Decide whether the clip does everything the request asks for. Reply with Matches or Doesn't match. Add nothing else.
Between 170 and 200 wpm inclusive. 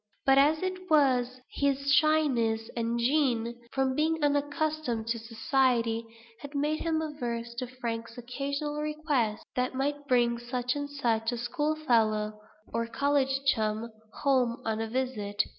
Doesn't match